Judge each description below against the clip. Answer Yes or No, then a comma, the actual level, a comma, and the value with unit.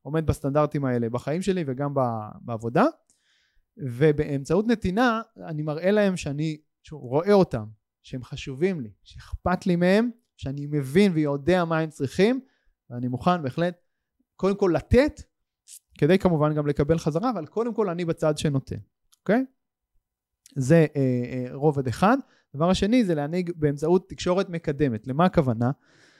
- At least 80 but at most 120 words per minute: No, average, 135 wpm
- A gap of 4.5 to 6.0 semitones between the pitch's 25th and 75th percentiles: Yes, average, 5.3 semitones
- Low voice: No, medium, 160 Hz